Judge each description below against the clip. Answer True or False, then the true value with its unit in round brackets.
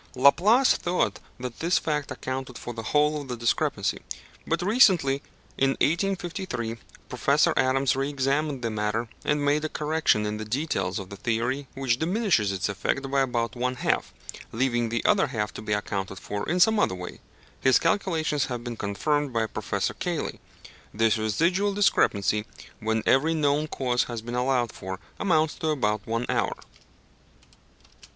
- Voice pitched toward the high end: False (130 Hz)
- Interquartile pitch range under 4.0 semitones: False (5.4 semitones)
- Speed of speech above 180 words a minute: False (160 wpm)